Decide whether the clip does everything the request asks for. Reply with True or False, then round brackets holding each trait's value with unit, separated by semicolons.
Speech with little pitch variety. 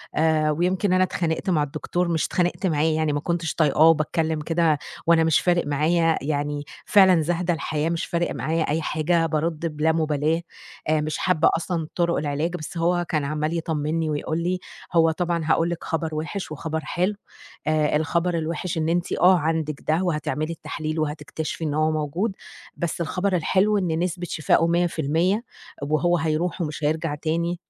True (2.0 semitones)